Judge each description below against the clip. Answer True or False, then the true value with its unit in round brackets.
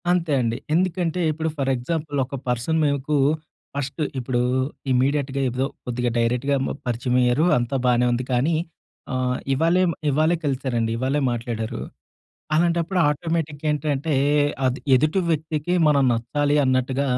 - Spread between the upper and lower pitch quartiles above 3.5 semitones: True (4.0 semitones)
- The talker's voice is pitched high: False (140 Hz)